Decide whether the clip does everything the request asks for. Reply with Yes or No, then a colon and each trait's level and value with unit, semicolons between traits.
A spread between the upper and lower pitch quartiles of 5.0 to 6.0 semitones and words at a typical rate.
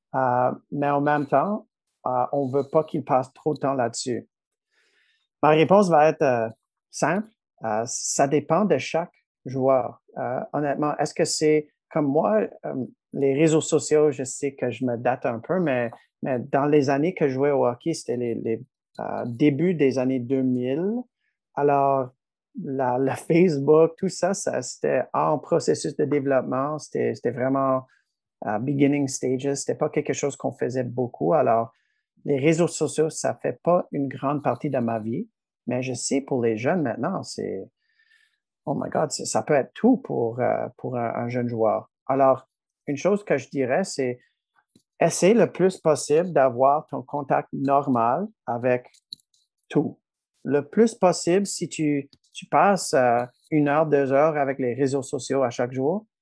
No: average, 3.5 semitones; average, 170 wpm